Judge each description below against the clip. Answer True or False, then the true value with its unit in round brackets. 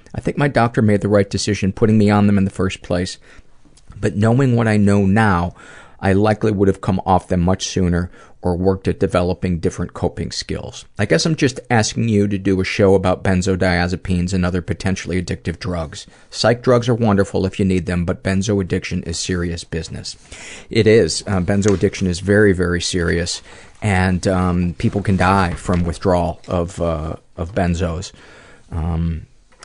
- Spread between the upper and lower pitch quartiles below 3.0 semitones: True (2.4 semitones)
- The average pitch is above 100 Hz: False (95 Hz)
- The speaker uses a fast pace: False (180 wpm)